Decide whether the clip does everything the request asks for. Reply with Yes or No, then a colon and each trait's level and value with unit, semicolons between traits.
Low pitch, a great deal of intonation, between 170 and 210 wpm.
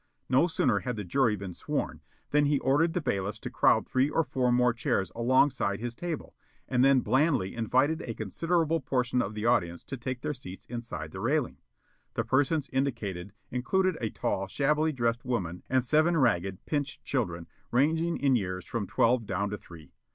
Yes: low, 125 Hz; wide, 5.7 semitones; average, 180 wpm